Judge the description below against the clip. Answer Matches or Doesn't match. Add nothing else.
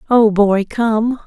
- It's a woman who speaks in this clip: Matches